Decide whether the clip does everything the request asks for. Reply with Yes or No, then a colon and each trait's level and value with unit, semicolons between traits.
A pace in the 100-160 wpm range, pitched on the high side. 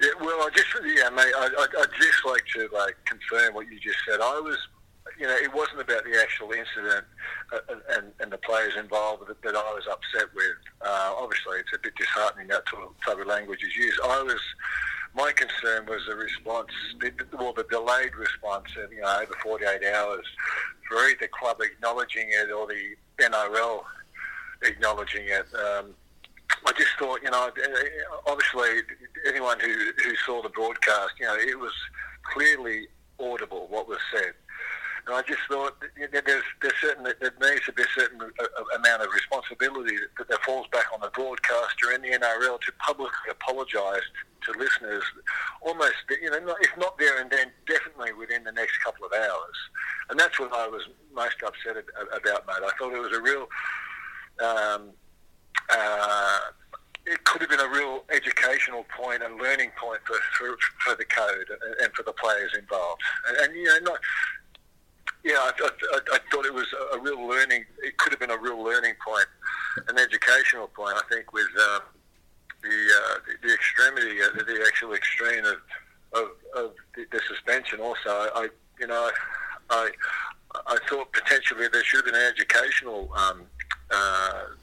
No: average, 175 wpm; very high, 395 Hz